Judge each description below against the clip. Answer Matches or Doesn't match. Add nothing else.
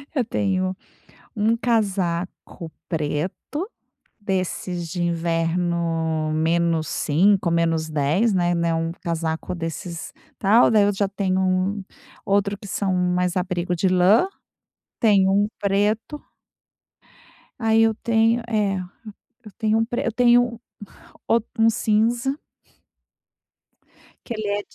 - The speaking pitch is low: Doesn't match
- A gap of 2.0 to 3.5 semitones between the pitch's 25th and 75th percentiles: Doesn't match